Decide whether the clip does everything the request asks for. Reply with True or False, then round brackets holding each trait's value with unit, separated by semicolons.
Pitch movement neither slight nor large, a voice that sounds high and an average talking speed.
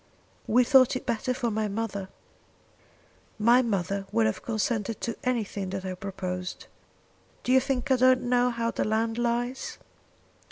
True (3.9 semitones; 230 Hz; 155 wpm)